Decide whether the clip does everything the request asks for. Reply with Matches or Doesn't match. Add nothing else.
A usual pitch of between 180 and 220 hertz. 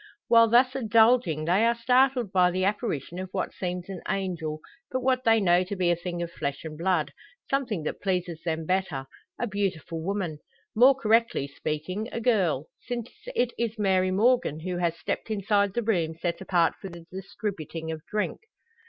Matches